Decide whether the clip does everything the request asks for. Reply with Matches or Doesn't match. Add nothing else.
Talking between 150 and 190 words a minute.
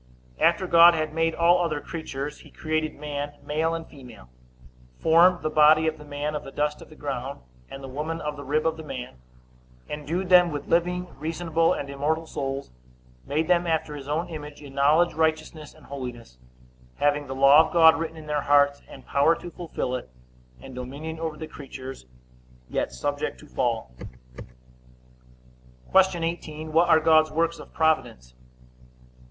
Matches